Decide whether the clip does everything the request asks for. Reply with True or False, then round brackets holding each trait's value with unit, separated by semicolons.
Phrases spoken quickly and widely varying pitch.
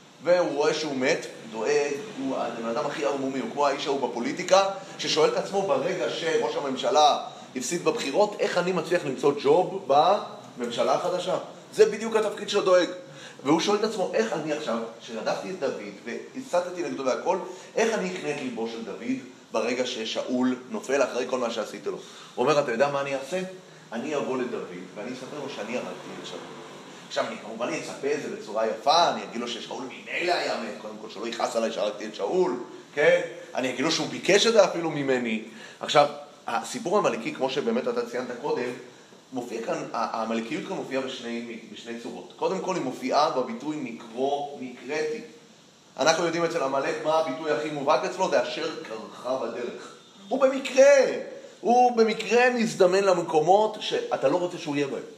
True (175 wpm; 7.7 semitones)